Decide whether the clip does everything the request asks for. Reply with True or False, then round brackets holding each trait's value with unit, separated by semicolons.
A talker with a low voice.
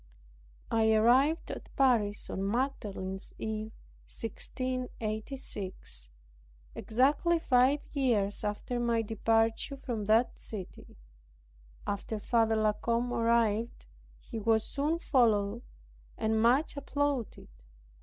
False (230 Hz)